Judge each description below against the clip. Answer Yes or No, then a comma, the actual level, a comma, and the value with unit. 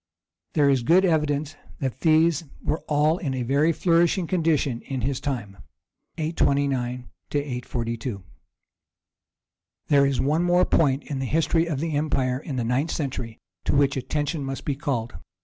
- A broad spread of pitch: No, average, 3.5 semitones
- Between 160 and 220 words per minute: No, average, 150 wpm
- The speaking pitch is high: No, medium, 140 Hz